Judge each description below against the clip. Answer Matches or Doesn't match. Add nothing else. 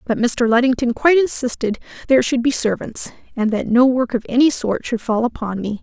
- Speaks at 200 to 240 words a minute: Matches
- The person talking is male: Doesn't match